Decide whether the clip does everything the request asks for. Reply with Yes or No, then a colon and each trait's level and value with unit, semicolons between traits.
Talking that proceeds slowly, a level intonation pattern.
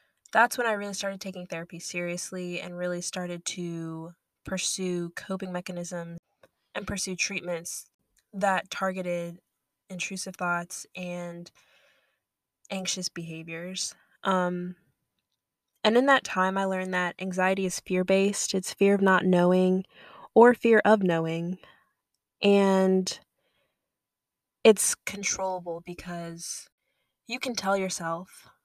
Yes: slow, 115 wpm; narrow, 1.7 semitones